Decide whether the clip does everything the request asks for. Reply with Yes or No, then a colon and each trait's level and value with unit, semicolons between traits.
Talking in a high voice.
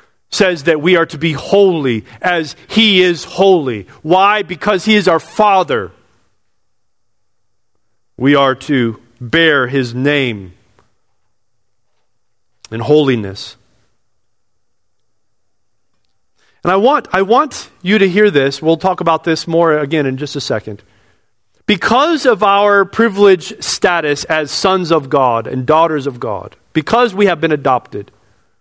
No: medium, 140 Hz